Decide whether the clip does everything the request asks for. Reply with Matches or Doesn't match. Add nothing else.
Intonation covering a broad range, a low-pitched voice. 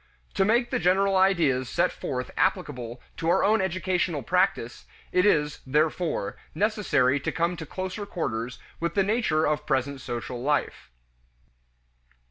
Doesn't match